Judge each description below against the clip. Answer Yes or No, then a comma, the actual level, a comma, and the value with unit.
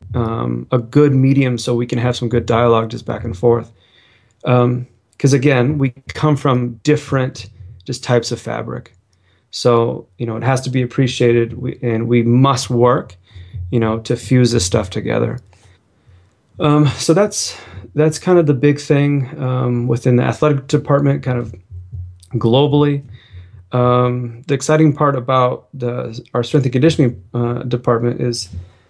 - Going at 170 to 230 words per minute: No, average, 155 wpm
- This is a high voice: No, low, 120 Hz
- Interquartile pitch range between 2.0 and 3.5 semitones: Yes, average, 2.9 semitones